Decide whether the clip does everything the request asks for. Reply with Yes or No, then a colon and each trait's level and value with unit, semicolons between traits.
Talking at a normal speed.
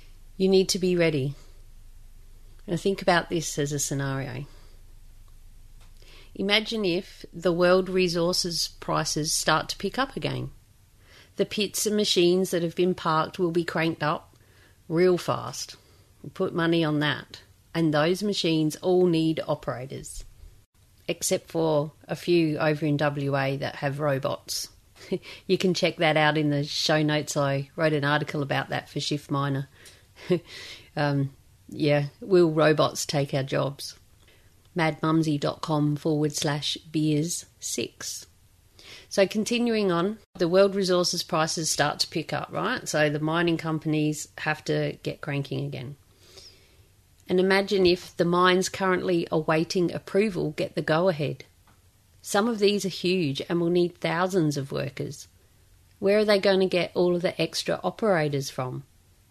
Yes: average, 145 wpm